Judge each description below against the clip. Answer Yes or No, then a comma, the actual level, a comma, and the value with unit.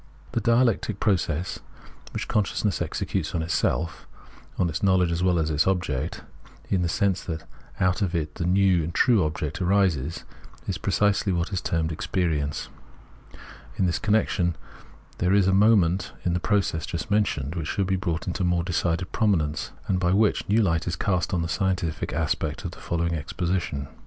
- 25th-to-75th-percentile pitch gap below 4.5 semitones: Yes, average, 2.9 semitones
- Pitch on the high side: No, very low, 90 Hz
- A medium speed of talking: Yes, average, 185 wpm